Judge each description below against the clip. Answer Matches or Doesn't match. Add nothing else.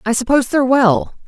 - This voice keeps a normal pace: Matches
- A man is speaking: Doesn't match